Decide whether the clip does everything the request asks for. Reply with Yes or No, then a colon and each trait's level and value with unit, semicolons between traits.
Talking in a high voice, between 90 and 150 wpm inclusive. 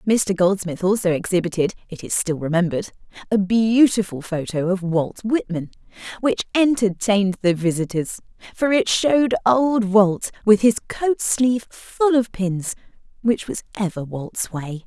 Yes: high, 200 Hz; average, 140 wpm